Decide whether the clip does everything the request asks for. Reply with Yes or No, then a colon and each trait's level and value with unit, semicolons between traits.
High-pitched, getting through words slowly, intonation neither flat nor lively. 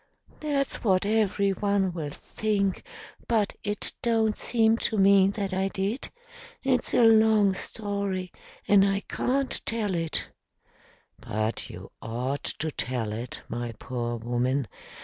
No: high, 195 Hz; slow, 130 wpm; wide, 7.4 semitones